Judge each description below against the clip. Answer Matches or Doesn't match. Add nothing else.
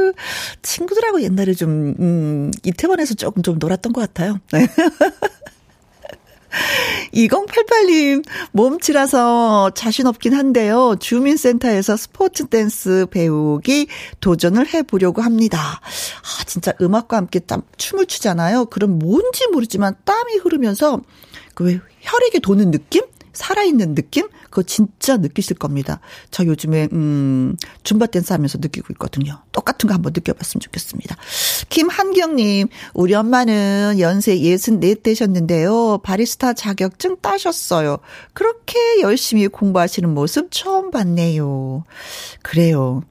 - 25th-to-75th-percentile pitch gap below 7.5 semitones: Doesn't match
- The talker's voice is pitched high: Matches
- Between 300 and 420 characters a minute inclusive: Doesn't match